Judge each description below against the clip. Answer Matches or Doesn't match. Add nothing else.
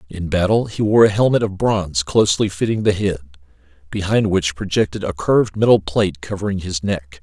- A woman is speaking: Doesn't match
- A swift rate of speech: Doesn't match